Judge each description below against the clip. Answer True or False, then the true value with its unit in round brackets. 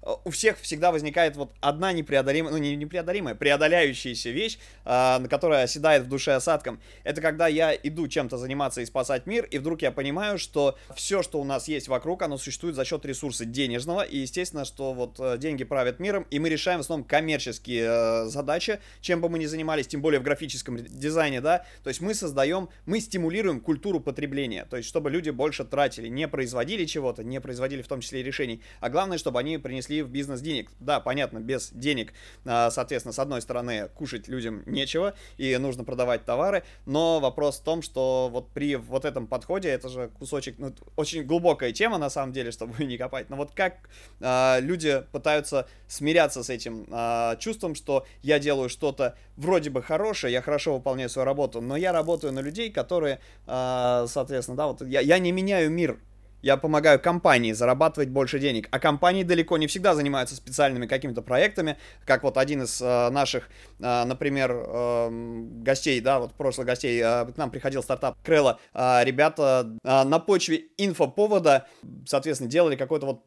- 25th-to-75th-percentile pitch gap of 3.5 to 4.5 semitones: True (4.0 semitones)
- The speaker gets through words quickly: True (180 wpm)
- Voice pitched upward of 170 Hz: False (140 Hz)